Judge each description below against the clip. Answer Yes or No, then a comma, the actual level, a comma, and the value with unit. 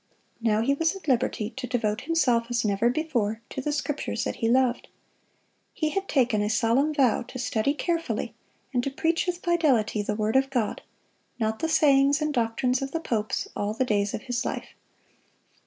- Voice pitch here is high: Yes, very high, 250 Hz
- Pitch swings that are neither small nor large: Yes, average, 4.9 semitones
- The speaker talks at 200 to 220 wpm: No, average, 190 wpm